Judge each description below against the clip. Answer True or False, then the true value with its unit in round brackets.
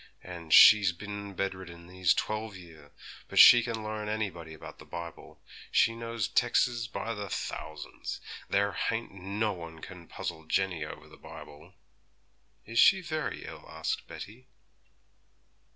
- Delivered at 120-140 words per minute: True (135 wpm)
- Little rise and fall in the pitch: False (4.6 semitones)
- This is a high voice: False (100 Hz)